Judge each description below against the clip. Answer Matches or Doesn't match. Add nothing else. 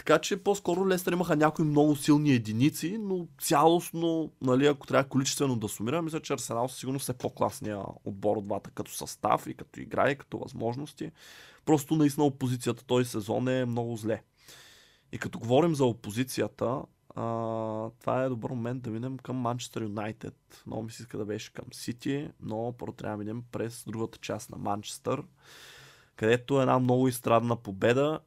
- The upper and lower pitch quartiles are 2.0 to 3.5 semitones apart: Doesn't match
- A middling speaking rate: Doesn't match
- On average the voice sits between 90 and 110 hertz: Doesn't match